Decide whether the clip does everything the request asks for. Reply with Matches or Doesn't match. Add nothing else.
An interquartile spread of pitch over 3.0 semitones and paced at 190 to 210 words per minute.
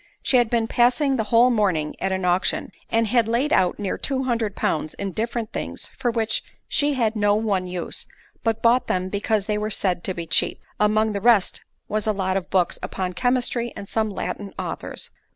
Matches